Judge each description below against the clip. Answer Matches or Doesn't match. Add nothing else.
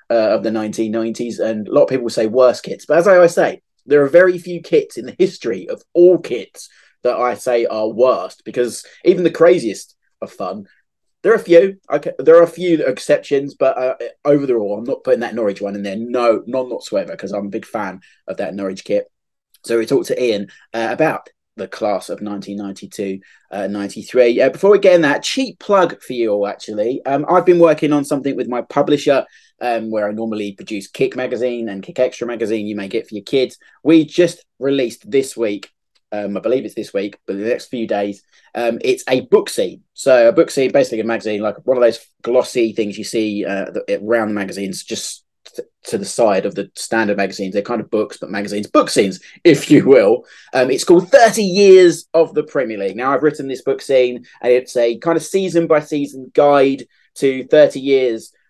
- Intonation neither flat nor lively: Doesn't match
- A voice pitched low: Matches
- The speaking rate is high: Matches